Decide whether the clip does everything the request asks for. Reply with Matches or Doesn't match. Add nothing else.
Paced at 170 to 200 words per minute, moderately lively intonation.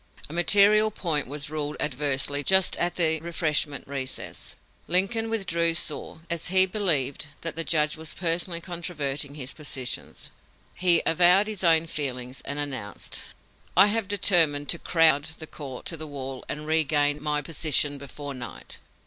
Doesn't match